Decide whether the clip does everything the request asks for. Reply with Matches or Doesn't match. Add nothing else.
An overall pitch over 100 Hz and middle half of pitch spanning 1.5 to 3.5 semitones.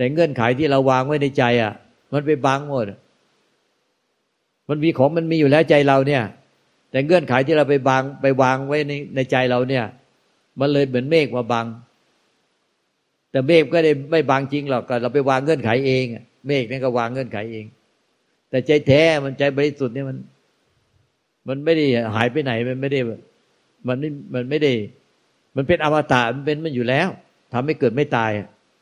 Matches